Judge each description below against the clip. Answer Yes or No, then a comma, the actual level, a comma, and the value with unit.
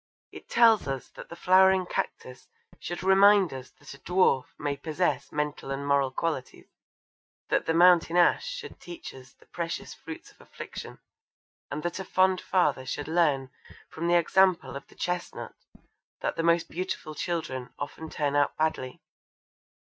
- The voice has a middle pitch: Yes, medium, 165 Hz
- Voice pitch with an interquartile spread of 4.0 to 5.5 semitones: Yes, average, 4.4 semitones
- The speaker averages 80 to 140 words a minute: No, average, 160 wpm